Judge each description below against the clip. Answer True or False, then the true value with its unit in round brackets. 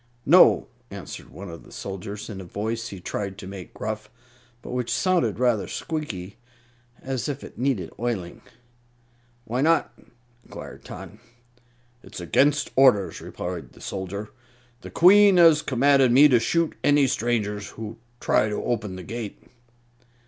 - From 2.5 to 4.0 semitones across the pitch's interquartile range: False (5.4 semitones)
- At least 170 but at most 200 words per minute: False (145 wpm)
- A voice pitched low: True (115 Hz)